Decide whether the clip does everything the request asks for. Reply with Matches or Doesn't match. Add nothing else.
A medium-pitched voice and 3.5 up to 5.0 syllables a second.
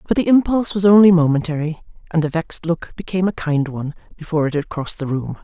Doesn't match